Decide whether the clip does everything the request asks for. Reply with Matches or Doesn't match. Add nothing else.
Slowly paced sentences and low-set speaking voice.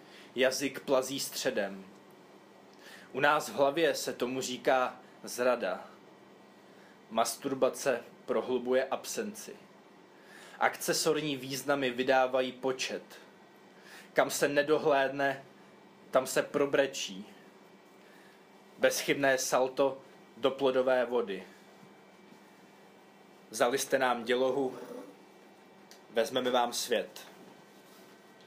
Matches